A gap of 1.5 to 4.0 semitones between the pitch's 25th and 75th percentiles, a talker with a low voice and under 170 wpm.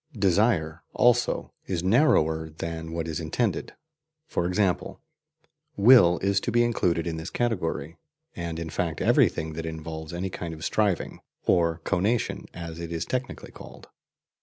Yes: average, 3.7 semitones; very low, 85 Hz; average, 150 wpm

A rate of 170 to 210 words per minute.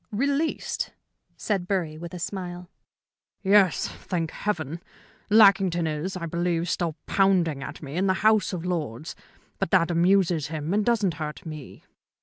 No: average, 145 wpm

